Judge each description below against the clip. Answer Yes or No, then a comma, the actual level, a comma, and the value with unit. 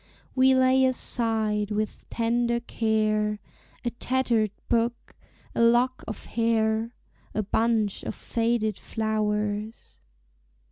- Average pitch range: No, narrow, 1.9 semitones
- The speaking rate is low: Yes, slow, 100 wpm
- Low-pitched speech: No, high, 225 Hz